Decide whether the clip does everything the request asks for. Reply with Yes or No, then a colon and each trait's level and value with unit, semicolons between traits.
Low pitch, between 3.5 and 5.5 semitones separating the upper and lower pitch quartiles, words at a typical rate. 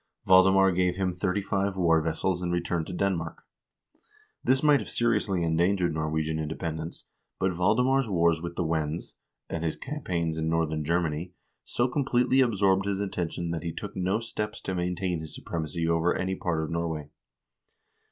No: very low, 90 Hz; average, 2.9 semitones; average, 170 wpm